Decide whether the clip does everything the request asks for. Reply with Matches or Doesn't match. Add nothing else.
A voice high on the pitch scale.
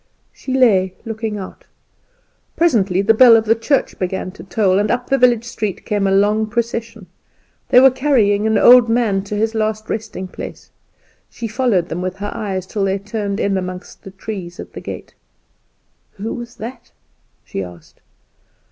Matches